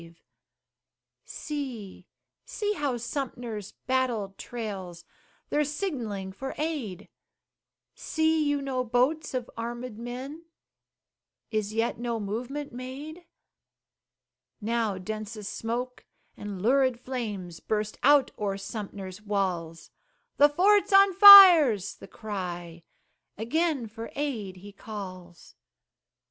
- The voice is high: Yes, high, 235 Hz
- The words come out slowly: Yes, slow, 105 wpm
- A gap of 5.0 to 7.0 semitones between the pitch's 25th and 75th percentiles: Yes, wide, 5.6 semitones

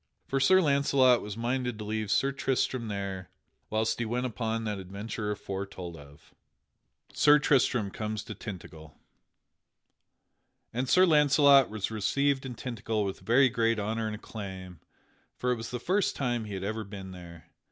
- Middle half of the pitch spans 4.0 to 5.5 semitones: Yes, average, 4.4 semitones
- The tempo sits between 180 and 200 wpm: No, average, 165 wpm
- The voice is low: Yes, low, 110 Hz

